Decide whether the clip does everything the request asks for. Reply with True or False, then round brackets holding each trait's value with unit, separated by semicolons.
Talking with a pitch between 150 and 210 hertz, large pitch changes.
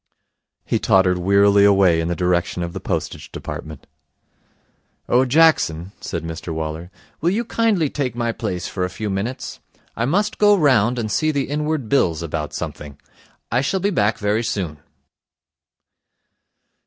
False (105 Hz; 8.0 semitones)